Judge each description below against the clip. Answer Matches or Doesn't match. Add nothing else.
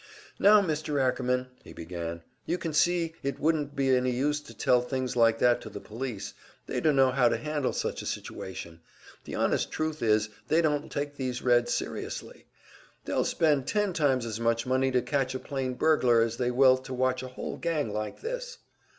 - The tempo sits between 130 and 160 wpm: Doesn't match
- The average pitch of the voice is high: Doesn't match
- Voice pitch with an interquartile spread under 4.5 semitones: Matches